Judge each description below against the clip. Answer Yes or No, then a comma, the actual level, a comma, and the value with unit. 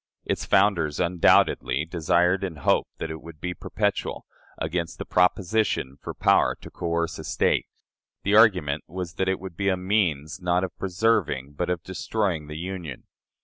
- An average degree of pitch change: Yes, average, 3.1 semitones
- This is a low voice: Yes, very low, 90 Hz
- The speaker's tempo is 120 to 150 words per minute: No, average, 165 wpm